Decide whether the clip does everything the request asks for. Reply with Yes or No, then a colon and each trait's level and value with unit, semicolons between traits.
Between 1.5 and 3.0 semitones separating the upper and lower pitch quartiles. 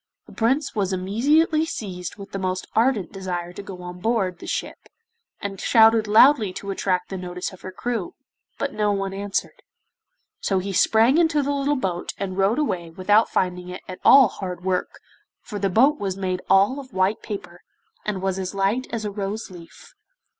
No: average, 3.6 semitones